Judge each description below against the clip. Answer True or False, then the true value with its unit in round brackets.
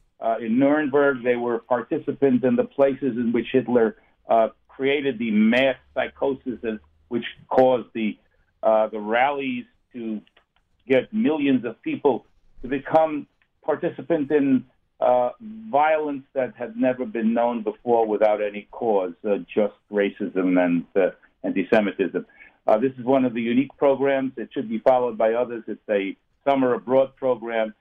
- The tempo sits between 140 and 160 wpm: True (150 wpm)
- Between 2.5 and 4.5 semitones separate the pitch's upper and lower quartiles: True (3.3 semitones)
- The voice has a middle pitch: False (125 Hz)